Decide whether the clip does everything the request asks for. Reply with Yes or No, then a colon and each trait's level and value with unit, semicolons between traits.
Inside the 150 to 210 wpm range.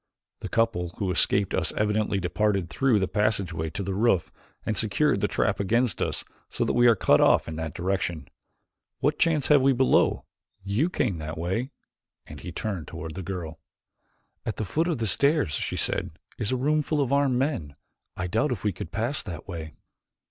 Yes: average, 195 wpm